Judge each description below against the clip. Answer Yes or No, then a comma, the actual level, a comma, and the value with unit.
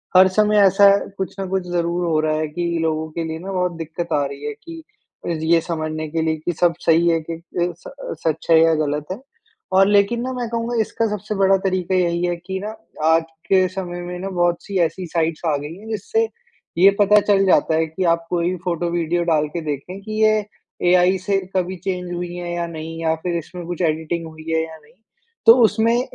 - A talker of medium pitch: Yes, medium, 175 Hz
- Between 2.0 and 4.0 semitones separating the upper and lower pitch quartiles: Yes, average, 3.0 semitones